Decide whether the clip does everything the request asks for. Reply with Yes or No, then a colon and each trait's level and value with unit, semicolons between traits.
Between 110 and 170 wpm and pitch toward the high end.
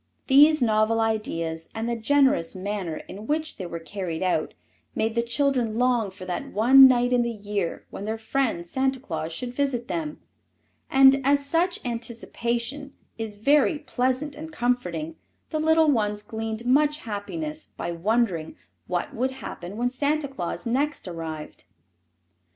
Yes: average, 150 wpm; high, 235 Hz